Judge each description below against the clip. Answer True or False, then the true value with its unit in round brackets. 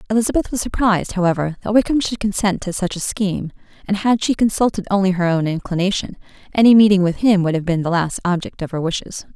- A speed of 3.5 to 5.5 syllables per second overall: False (6.4 syllables/s)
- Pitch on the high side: True (195 Hz)